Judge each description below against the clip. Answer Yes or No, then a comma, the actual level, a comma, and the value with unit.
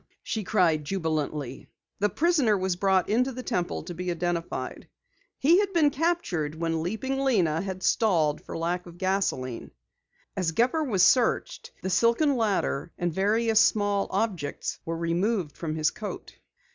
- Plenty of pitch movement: Yes, wide, 5.8 semitones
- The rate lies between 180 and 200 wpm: No, average, 150 wpm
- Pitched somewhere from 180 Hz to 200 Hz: Yes, high, 190 Hz